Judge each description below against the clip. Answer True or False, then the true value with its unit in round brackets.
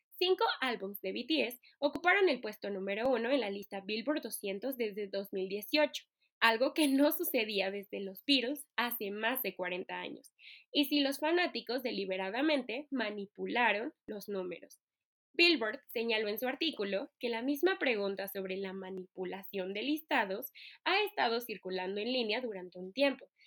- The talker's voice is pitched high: True (230 Hz)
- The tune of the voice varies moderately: False (6.4 semitones)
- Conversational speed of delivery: True (150 wpm)